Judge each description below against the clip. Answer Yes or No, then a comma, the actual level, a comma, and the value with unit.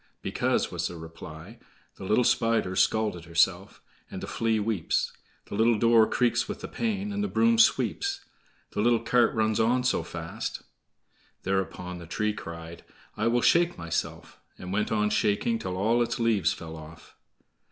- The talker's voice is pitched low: Yes, low, 110 Hz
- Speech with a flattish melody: No, average, 4.7 semitones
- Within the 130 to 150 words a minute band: No, average, 165 wpm